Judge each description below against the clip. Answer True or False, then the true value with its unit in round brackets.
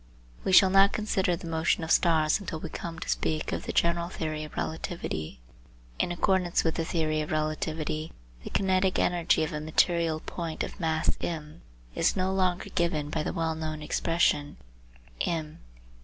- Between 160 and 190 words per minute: True (170 wpm)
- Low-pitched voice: False (165 Hz)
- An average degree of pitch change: False (2.1 semitones)